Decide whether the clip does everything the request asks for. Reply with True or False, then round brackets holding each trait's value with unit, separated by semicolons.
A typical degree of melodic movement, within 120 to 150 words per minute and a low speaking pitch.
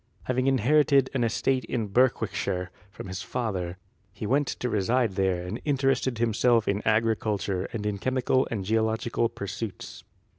True (4.3 semitones; 145 wpm; 115 Hz)